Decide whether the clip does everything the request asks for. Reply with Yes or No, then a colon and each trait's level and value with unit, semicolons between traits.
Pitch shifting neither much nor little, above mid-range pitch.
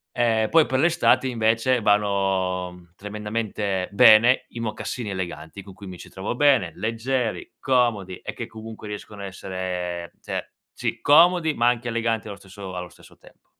No: average, 4.0 semitones; low, 105 Hz